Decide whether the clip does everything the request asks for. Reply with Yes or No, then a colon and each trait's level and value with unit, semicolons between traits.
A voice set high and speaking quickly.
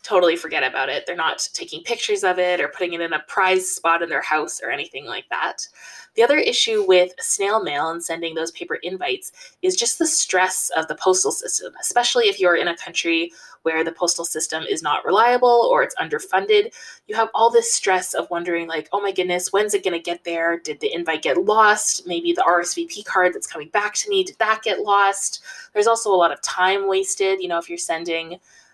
Yes: high, 195 Hz; fast, 220 wpm